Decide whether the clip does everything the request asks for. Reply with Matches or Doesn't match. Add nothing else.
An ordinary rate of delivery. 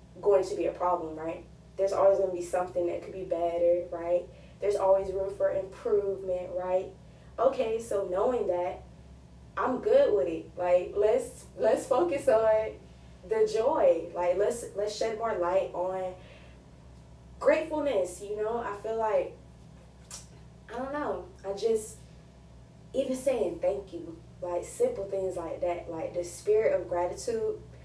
Matches